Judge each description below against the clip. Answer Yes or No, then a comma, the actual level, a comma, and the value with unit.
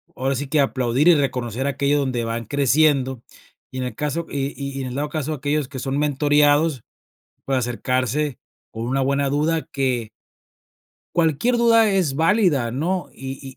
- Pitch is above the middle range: No, medium, 140 Hz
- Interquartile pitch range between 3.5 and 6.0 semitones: No, average, 2.7 semitones